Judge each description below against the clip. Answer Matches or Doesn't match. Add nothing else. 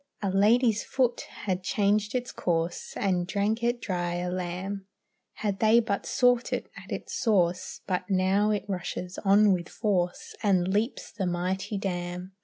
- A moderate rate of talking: Matches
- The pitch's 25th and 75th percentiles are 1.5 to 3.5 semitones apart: Matches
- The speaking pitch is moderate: Doesn't match